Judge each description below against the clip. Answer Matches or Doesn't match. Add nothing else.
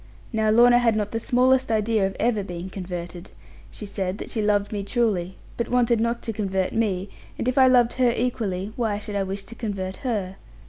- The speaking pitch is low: Doesn't match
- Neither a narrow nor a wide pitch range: Matches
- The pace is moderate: Doesn't match